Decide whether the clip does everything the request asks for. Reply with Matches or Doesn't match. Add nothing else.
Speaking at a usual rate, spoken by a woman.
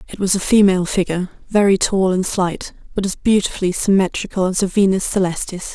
Matches